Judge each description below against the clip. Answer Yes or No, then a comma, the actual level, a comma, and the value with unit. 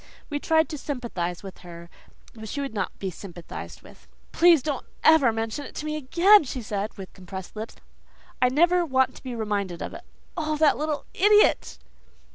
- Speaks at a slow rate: No, average, 185 wpm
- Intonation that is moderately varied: No, wide, 7.2 semitones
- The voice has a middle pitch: No, very high, 255 Hz